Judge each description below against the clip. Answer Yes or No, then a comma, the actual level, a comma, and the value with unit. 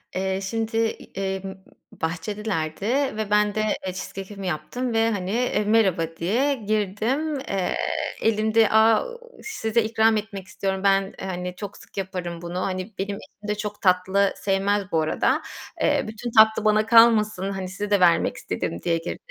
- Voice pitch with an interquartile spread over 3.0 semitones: No, narrow, 2.6 semitones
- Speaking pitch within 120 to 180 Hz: No, high, 205 Hz